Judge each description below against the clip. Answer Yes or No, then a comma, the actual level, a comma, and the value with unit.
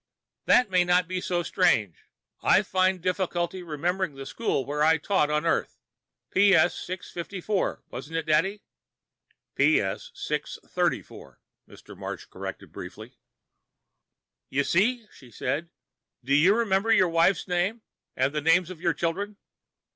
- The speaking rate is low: Yes, slow, 130 wpm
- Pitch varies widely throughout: No, average, 3.9 semitones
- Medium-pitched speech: Yes, medium, 175 Hz